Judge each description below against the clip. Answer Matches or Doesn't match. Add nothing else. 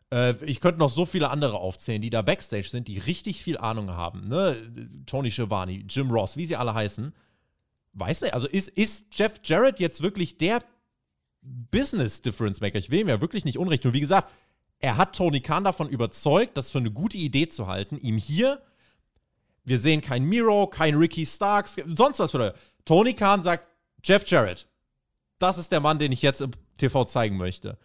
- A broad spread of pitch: Matches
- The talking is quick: Matches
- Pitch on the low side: Doesn't match